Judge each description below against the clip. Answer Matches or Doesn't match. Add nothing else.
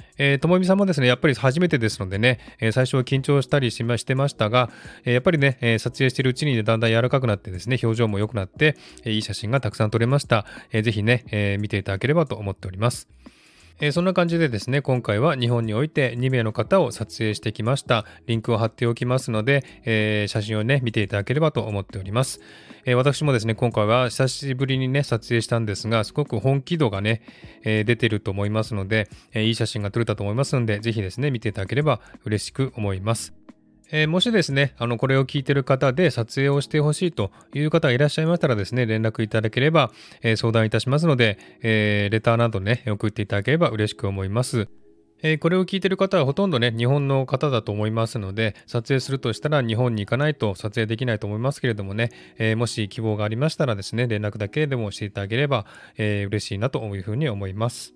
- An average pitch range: Matches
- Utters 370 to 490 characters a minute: Matches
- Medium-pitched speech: Doesn't match